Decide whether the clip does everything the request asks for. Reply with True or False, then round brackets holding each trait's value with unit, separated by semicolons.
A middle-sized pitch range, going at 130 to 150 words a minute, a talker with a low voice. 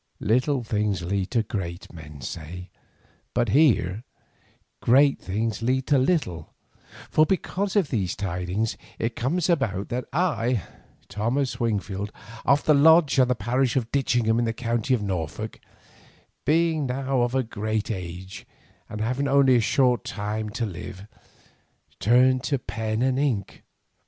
True (4.7 semitones; 145 wpm; 115 Hz)